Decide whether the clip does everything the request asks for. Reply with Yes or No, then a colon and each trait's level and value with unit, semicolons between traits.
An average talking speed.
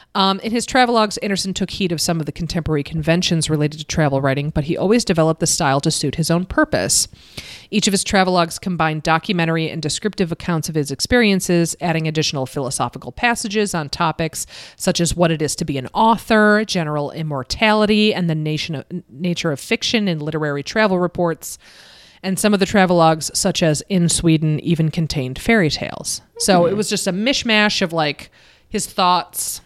Yes: average, 185 wpm